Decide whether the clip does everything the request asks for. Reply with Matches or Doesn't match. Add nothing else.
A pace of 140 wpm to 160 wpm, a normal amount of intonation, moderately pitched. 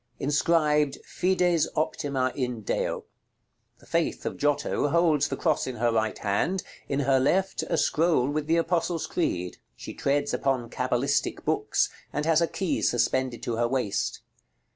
Matches